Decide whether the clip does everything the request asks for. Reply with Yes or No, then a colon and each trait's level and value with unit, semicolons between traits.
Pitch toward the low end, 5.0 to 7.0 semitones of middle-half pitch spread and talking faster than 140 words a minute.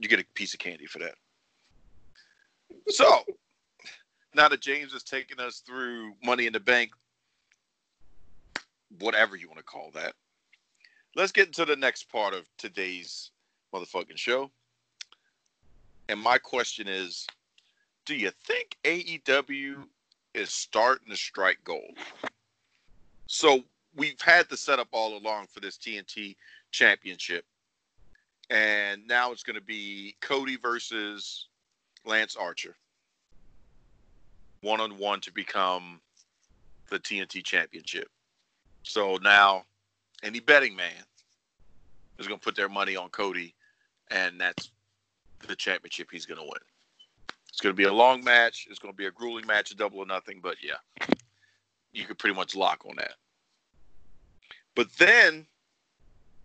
No: low, 115 Hz; average, 5.3 semitones; slow, 135 wpm